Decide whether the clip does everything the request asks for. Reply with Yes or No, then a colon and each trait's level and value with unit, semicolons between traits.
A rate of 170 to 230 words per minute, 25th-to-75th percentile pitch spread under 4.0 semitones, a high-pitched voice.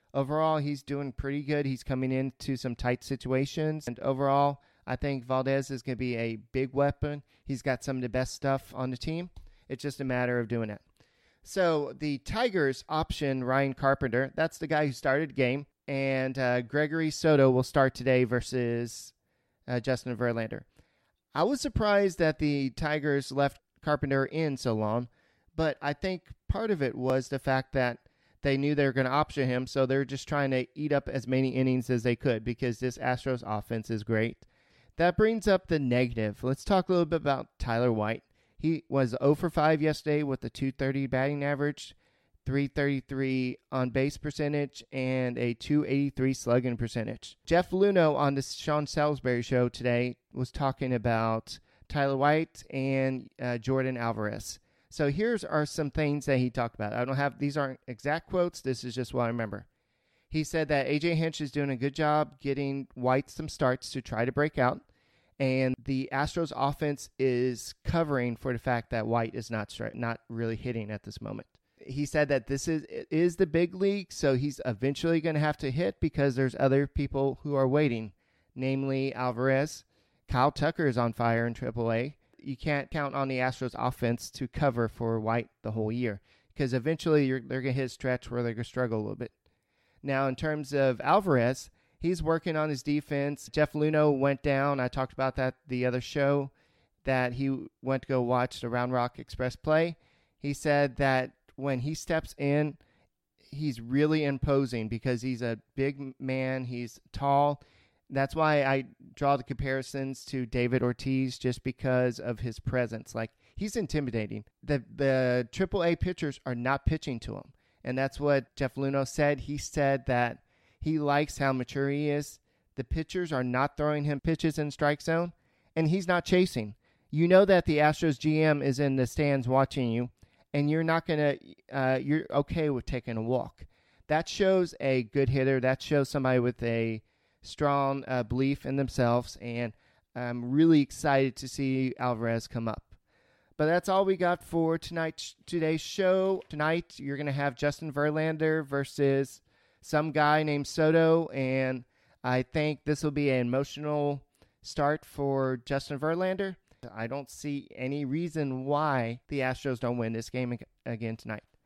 No: average, 180 wpm; average, 2.9 semitones; low, 135 Hz